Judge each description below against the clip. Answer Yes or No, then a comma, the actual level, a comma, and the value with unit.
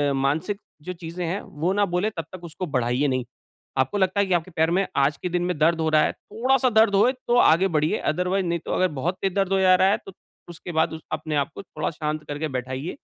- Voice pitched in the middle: Yes, medium, 170 Hz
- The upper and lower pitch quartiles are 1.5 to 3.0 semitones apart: No, average, 3.9 semitones